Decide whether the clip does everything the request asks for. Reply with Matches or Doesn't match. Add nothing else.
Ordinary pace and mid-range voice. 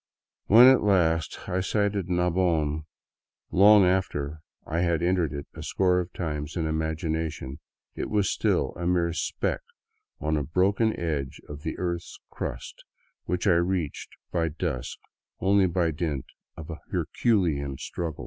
Doesn't match